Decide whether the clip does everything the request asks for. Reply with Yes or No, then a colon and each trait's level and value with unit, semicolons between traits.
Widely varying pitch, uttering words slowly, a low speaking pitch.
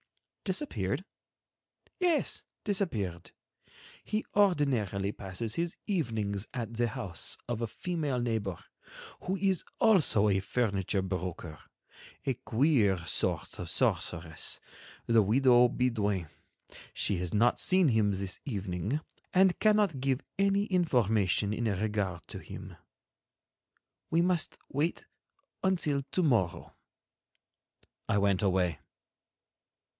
Yes: wide, 8.8 semitones; slow, 110 wpm; low, 115 Hz